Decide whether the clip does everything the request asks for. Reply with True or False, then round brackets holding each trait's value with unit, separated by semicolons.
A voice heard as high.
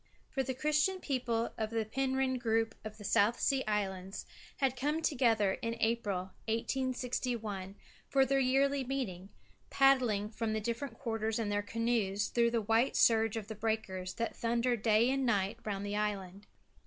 True (230 Hz)